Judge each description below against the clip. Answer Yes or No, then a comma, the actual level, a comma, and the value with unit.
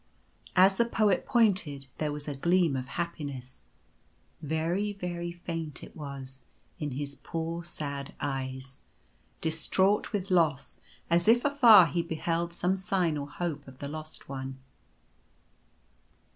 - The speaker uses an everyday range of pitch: Yes, average, 4.3 semitones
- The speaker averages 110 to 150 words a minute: Yes, average, 140 wpm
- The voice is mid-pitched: Yes, medium, 160 Hz